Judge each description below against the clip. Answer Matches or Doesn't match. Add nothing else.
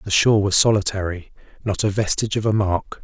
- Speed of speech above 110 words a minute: Matches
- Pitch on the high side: Doesn't match